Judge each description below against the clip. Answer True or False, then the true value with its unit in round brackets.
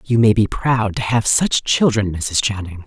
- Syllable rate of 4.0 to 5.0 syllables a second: True (4.3 syllables/s)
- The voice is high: False (110 Hz)